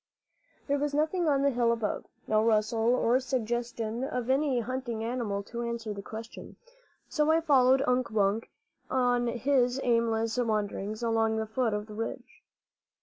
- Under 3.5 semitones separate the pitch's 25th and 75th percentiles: Yes, narrow, 2.6 semitones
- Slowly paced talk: No, average, 155 wpm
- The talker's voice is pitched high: Yes, high, 235 Hz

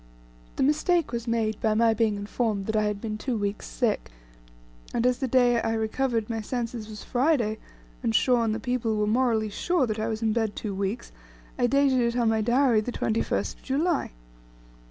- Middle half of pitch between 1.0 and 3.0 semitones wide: Yes, narrow, 2.6 semitones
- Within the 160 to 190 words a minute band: No, average, 200 wpm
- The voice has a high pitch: Yes, high, 230 Hz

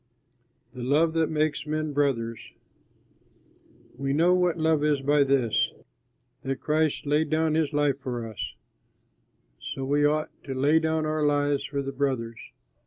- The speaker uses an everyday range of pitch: No, narrow, 2.3 semitones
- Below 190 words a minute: Yes, average, 150 wpm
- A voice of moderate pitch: Yes, medium, 145 Hz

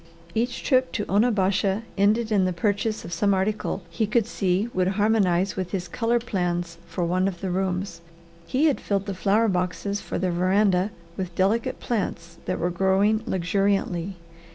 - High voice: Yes, high, 195 Hz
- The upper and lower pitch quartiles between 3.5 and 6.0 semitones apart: No, average, 2.8 semitones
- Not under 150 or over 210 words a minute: Yes, average, 170 wpm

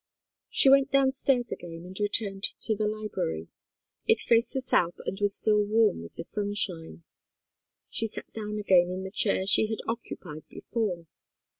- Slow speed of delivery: No, average, 160 wpm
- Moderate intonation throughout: Yes, average, 3.7 semitones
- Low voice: No, high, 205 Hz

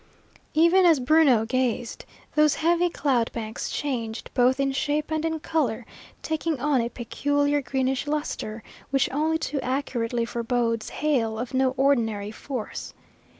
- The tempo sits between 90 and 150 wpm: Yes, average, 140 wpm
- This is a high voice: Yes, very high, 265 Hz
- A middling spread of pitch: Yes, average, 4.3 semitones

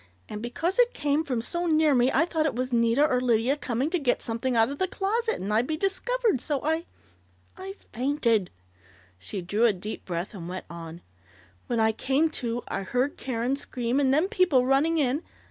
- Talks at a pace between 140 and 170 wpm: No, fast, 205 wpm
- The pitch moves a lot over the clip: Yes, wide, 5.7 semitones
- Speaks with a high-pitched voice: Yes, very high, 255 Hz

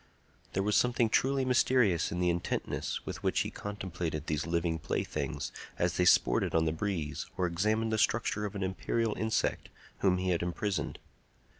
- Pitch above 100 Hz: No, very low, 95 Hz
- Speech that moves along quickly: No, average, 170 wpm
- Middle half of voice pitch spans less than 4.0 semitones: No, average, 4.3 semitones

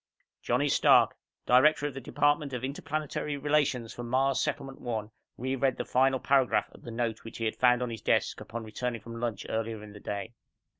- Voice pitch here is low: Yes, low, 125 Hz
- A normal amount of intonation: Yes, average, 3.1 semitones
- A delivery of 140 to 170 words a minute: No, average, 200 wpm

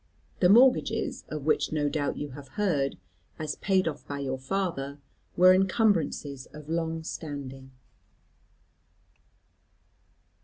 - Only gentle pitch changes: No, average, 4.6 semitones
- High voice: No, medium, 155 Hz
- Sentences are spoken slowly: Yes, slow, 115 wpm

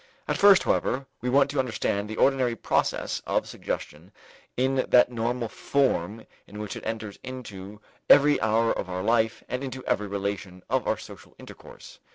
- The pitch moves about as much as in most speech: Yes, average, 4.1 semitones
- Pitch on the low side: Yes, low, 115 Hz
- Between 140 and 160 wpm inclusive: No, average, 170 wpm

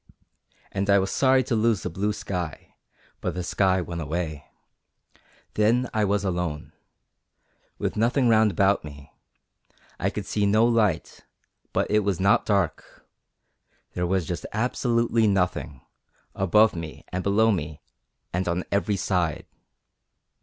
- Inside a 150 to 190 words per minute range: No, average, 140 wpm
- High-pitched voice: No, low, 100 Hz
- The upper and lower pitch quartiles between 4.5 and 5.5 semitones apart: No, average, 3.5 semitones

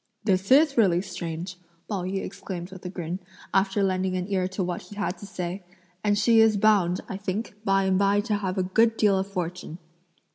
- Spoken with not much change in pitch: Yes, narrow, 2.0 semitones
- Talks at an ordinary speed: No, fast, 215 wpm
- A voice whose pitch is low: No, high, 195 Hz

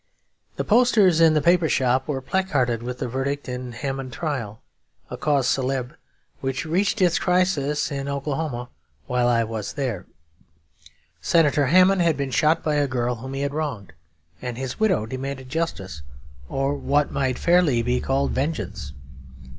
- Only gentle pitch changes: No, average, 4.0 semitones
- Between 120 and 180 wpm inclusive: Yes, average, 160 wpm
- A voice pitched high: No, low, 135 Hz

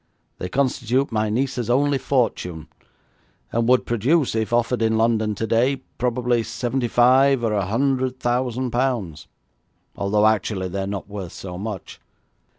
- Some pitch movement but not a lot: Yes, average, 3.3 semitones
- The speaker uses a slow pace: No, average, 145 wpm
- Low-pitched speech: Yes, low, 115 Hz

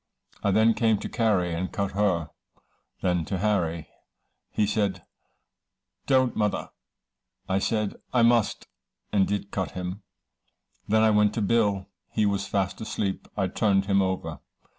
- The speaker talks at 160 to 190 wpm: No, average, 145 wpm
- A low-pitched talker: Yes, low, 100 Hz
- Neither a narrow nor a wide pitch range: No, narrow, 2.3 semitones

